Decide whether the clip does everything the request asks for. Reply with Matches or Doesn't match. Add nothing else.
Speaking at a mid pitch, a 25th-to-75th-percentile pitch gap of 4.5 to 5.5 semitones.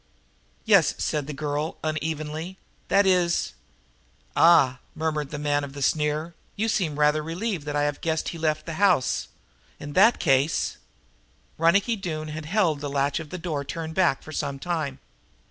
Doesn't match